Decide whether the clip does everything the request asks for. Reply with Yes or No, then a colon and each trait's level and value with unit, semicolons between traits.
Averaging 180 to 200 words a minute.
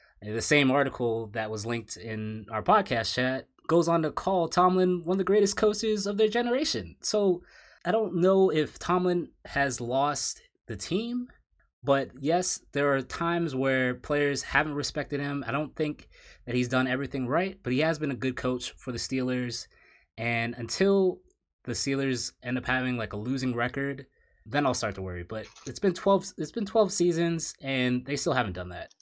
Yes: average, 190 wpm